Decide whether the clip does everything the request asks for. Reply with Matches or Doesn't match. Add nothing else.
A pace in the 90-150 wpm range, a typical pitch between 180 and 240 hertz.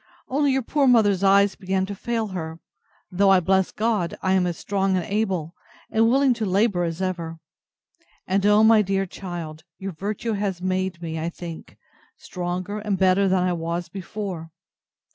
Doesn't match